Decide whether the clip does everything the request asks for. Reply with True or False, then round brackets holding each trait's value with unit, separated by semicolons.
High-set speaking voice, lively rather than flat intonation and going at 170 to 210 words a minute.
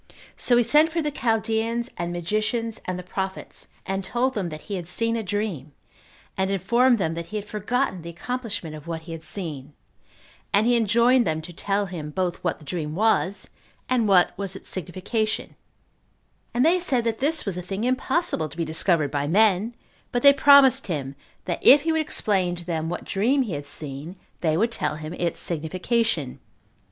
True (195 Hz; 5.7 semitones; 195 wpm)